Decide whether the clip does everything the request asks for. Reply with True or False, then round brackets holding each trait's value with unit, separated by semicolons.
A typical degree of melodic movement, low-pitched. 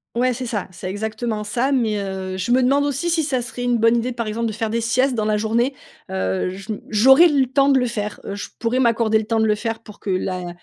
False (3.2 semitones; 230 Hz)